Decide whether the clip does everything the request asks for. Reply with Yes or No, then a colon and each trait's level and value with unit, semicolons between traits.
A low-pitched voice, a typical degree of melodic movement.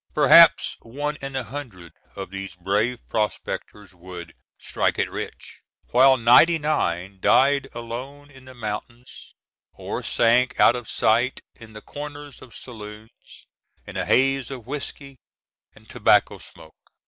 Yes: low, 120 Hz; average, 4.4 semitones